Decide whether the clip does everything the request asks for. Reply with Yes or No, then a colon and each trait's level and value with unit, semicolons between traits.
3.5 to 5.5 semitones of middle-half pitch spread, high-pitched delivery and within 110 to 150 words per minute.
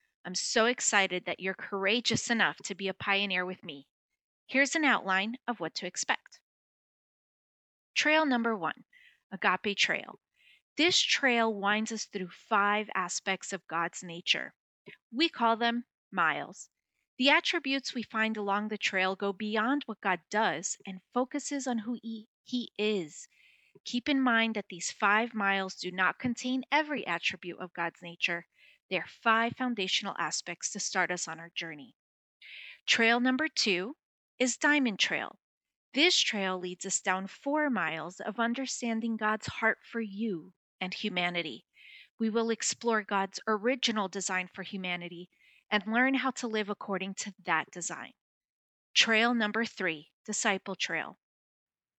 Yes: average, 4.4 semitones; high, 210 Hz; average, 145 wpm